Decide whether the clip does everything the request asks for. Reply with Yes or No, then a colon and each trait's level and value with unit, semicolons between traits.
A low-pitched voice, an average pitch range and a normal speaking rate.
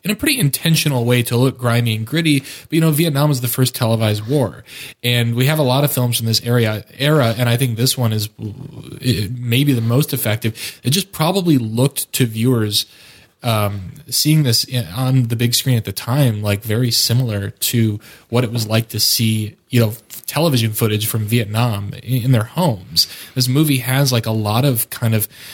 Yes: low, 120 Hz; average, 3.4 semitones; average, 195 wpm